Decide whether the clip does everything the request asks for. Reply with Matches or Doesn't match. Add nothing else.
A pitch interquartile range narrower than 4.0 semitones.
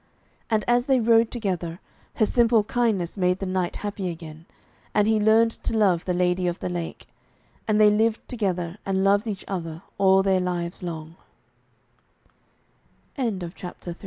Matches